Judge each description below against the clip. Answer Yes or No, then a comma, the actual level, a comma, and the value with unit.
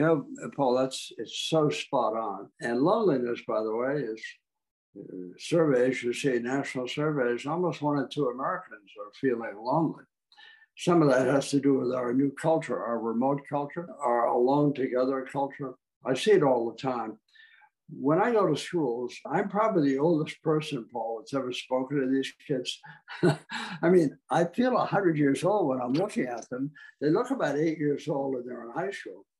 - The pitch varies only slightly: No, average, 4.2 semitones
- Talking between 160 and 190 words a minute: Yes, average, 185 wpm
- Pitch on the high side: No, medium, 140 Hz